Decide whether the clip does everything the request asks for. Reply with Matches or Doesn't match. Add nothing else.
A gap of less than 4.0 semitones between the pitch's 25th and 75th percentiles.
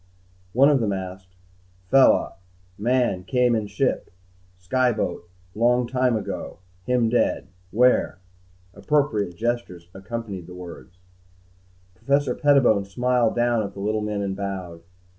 Doesn't match